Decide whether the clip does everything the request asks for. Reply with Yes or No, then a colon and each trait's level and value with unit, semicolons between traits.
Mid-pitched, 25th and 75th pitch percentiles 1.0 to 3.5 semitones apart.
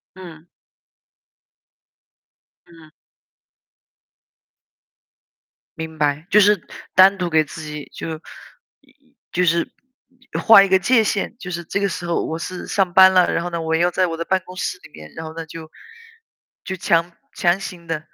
Yes: medium, 175 Hz; average, 2.7 semitones